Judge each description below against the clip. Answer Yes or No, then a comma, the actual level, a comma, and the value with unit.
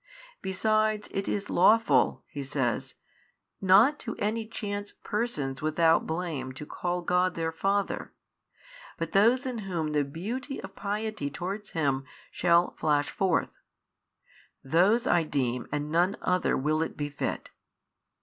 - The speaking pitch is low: No, medium, 180 Hz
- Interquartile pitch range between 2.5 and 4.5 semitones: No, wide, 5.5 semitones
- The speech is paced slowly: Yes, slow, 130 wpm